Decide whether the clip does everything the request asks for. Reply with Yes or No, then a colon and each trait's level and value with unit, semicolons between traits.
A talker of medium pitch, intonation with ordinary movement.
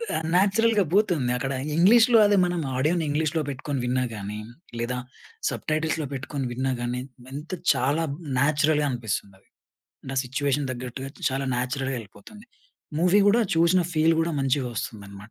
Yes: medium, 145 Hz; average, 4.9 semitones